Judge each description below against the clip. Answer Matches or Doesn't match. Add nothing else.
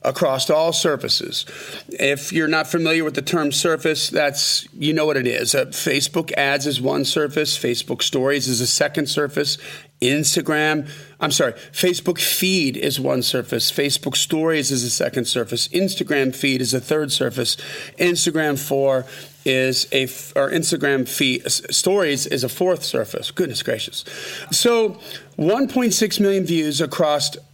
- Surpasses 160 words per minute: Doesn't match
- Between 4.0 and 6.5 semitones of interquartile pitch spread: Doesn't match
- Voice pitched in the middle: Matches